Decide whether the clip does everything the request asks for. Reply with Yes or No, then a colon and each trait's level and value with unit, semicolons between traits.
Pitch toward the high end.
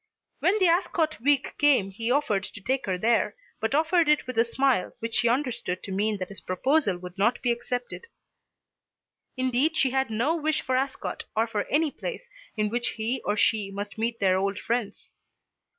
Yes: high, 240 Hz